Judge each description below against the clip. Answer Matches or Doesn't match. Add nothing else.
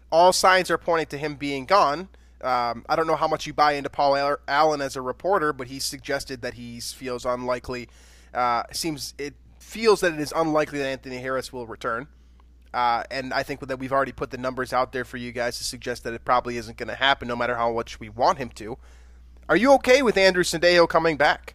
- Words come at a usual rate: Doesn't match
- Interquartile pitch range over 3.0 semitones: Matches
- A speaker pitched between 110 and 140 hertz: Matches